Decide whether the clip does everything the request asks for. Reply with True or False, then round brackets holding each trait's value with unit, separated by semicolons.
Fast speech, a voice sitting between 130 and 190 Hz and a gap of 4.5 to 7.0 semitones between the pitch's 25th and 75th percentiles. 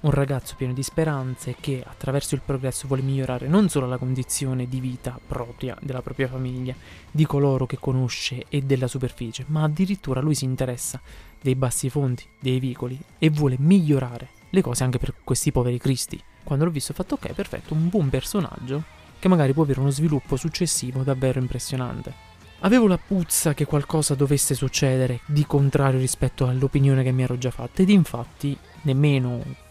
False (175 wpm; 135 Hz; 2.4 semitones)